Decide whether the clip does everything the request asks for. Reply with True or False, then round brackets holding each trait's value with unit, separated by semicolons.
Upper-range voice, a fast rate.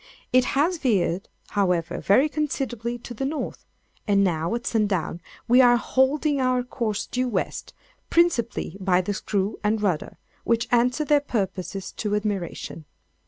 False (230 Hz; 145 wpm)